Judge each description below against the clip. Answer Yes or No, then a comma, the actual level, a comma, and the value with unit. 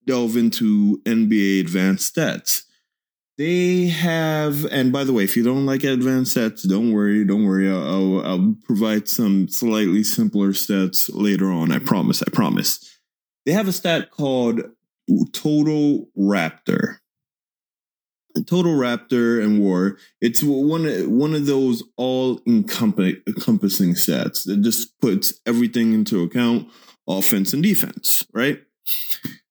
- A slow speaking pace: Yes, slow, 130 wpm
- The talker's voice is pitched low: Yes, low, 120 Hz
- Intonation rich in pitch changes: Yes, wide, 6.4 semitones